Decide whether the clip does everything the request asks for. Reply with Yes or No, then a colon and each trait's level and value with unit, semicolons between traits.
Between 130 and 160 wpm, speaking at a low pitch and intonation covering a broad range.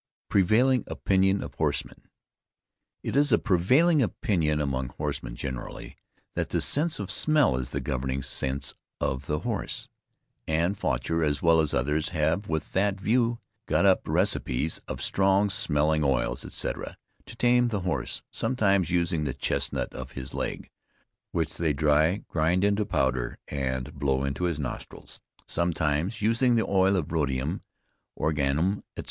Yes: average, 150 wpm; very low, 80 Hz; wide, 6.1 semitones